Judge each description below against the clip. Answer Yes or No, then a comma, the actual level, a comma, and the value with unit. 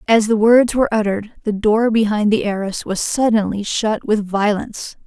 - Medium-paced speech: Yes, average, 180 wpm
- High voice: Yes, high, 215 Hz